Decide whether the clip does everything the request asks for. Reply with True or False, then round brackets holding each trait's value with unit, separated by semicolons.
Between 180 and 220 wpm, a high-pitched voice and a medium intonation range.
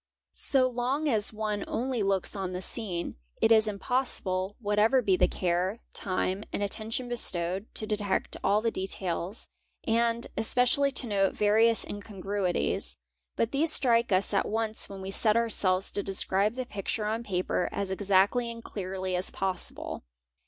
False (160 wpm; 205 Hz; 3.3 semitones)